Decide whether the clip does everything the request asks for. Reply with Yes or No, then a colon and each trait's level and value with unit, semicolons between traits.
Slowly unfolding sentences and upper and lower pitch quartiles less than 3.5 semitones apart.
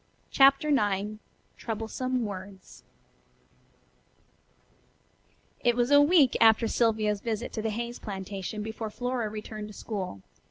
Yes: slow, 115 wpm; narrow, 2.6 semitones